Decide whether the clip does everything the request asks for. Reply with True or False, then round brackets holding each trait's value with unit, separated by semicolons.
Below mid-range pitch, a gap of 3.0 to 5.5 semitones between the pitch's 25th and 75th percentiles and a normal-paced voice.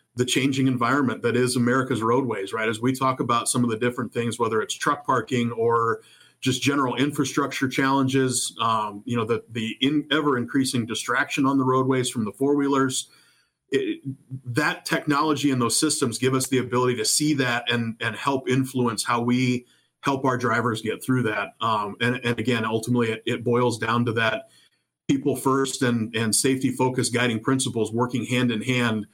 False (125 Hz; 2.4 semitones; 185 wpm)